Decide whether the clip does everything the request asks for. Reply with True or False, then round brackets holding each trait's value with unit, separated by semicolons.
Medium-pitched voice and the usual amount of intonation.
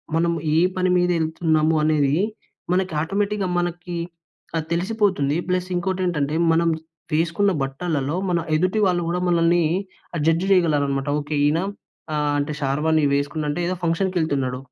True (165 Hz; 3.2 semitones)